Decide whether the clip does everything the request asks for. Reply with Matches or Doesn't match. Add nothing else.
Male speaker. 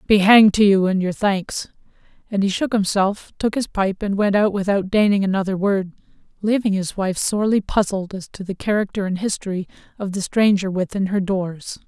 Doesn't match